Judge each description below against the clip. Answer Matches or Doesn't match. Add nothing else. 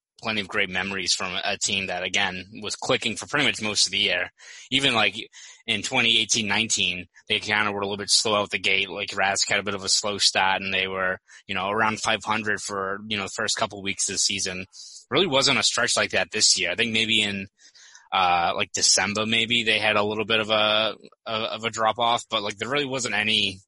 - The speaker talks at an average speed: Doesn't match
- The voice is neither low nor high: Doesn't match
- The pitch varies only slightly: Matches